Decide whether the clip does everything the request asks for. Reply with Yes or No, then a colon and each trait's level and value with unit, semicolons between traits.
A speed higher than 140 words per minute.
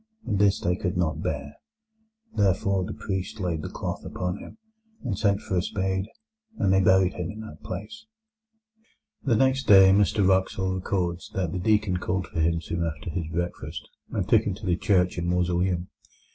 Yes: average, 185 wpm